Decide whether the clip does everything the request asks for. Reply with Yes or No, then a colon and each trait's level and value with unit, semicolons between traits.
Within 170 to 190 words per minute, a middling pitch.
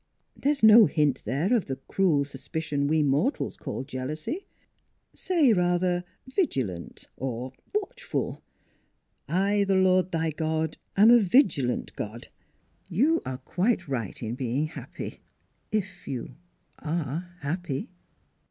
No: slow, 135 wpm; medium, 160 Hz